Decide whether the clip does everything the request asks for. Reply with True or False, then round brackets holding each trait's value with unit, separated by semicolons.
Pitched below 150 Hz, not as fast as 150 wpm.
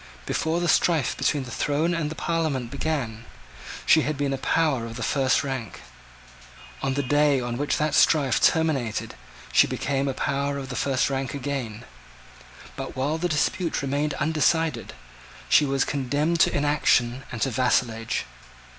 False (140 Hz; 160 wpm)